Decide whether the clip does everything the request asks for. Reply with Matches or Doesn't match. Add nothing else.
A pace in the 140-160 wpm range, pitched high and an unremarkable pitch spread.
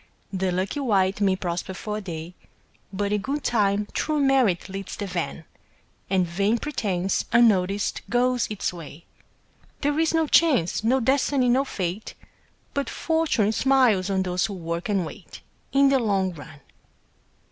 Doesn't match